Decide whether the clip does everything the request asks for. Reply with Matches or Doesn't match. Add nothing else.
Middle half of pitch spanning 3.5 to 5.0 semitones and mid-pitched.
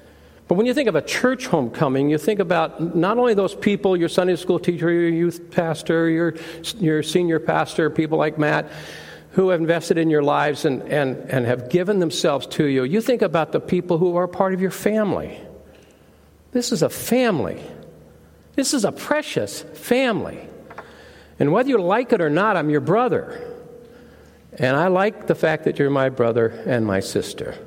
Matches